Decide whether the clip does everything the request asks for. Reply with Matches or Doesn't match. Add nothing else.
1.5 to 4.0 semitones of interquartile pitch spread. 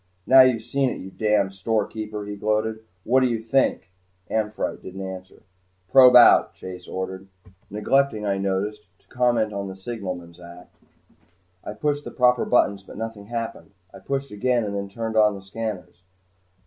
Matches